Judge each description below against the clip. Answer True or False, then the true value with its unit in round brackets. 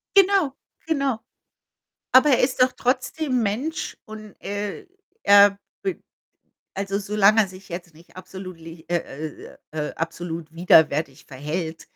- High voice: True (195 Hz)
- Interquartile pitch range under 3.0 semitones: False (7.2 semitones)